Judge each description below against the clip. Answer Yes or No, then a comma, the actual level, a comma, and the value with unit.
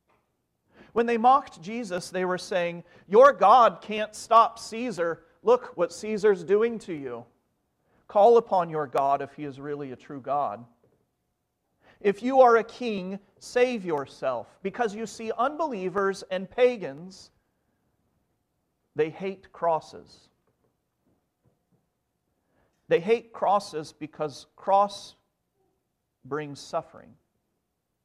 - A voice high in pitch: Yes, high, 195 Hz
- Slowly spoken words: Yes, slow, 110 wpm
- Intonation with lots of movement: Yes, wide, 5.9 semitones